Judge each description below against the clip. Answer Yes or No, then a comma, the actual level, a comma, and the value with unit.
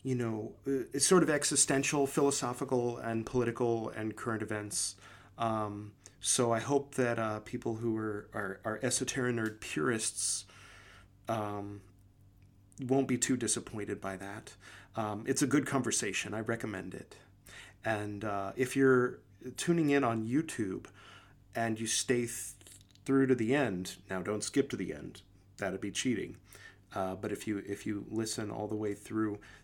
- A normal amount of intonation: Yes, average, 3.9 semitones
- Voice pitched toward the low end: Yes, low, 110 Hz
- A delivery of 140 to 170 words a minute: Yes, average, 155 wpm